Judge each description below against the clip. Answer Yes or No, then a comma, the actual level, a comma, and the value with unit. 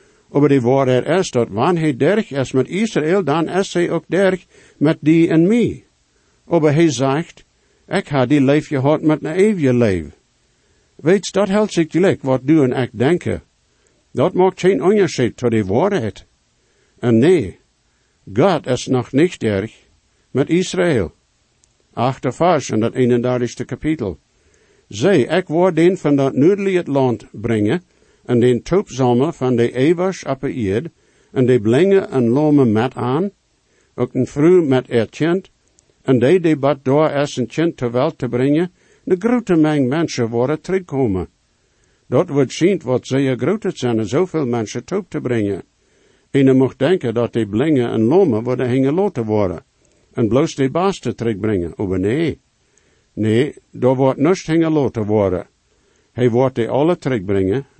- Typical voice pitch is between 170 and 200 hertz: No, low, 135 Hz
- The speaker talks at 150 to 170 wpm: Yes, average, 155 wpm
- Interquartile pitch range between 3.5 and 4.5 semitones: No, wide, 5.6 semitones